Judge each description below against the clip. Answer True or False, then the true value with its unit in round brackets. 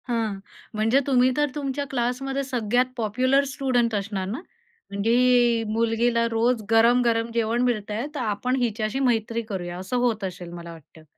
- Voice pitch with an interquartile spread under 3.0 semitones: True (2.6 semitones)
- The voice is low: False (230 Hz)